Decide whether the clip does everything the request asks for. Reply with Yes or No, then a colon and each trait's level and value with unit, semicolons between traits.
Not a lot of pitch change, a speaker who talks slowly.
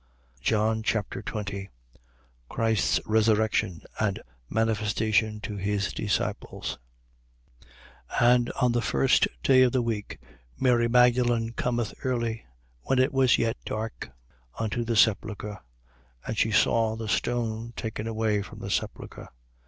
Yes: narrow, 1.8 semitones; slow, 125 wpm